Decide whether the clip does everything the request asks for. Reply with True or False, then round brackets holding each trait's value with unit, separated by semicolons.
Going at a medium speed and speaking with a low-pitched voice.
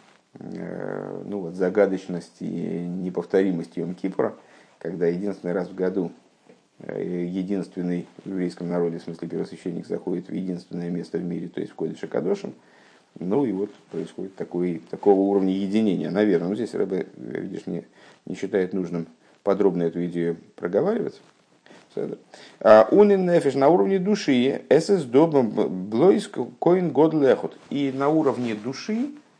True (130 wpm; 95 Hz)